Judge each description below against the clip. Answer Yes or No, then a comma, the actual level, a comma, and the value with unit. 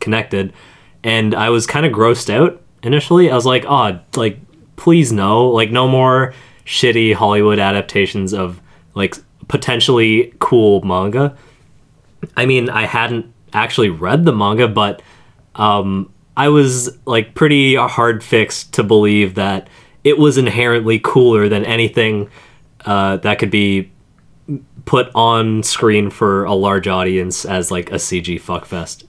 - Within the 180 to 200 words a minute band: No, average, 140 wpm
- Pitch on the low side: Yes, low, 115 Hz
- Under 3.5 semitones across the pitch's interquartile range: No, average, 4.0 semitones